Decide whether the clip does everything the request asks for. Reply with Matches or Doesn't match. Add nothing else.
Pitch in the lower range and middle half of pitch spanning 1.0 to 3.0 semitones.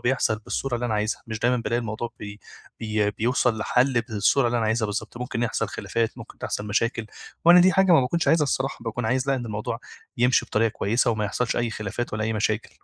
Matches